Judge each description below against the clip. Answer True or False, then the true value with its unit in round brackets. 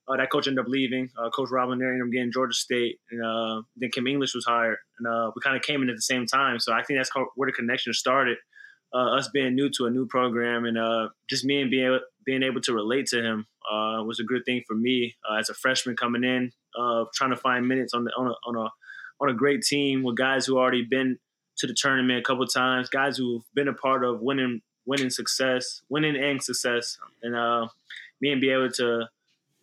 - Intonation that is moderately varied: False (2.0 semitones)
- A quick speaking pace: True (245 wpm)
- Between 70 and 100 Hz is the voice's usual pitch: False (125 Hz)